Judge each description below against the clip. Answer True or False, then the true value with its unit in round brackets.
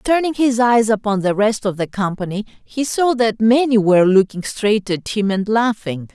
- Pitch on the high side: True (215 Hz)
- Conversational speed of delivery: True (195 wpm)